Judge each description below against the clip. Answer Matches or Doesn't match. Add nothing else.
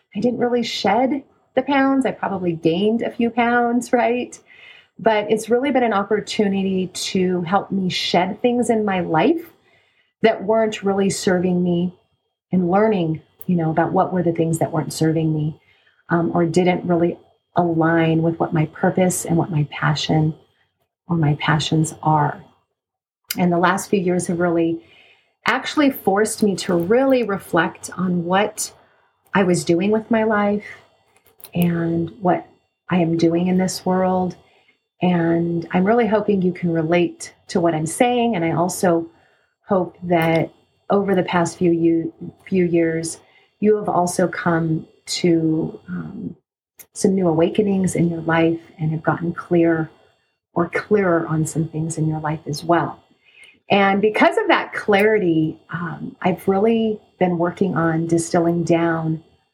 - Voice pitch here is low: Doesn't match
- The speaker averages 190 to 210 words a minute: Doesn't match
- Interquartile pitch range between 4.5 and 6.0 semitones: Doesn't match